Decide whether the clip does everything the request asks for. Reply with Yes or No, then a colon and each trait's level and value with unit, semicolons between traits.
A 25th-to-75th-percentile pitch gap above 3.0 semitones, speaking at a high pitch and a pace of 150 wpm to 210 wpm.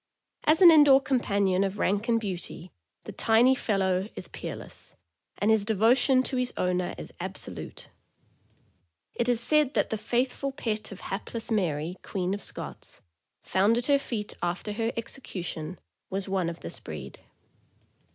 Yes: average, 4.7 semitones; high, 215 Hz; average, 155 wpm